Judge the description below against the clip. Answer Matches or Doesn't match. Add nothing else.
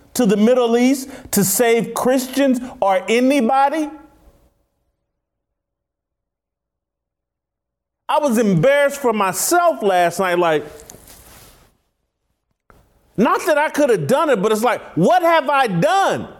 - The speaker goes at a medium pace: Doesn't match